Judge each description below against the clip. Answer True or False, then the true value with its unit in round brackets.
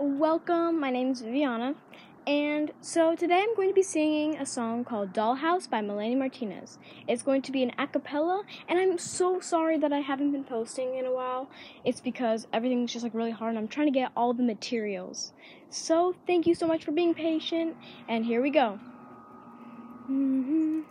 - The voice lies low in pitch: False (275 Hz)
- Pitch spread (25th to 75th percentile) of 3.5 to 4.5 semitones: False (4.9 semitones)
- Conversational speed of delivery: True (190 wpm)